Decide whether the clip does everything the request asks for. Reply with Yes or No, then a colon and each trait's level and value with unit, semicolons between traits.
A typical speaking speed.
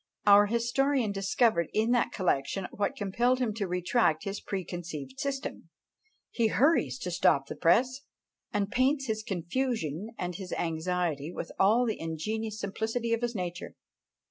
Yes: average, 145 wpm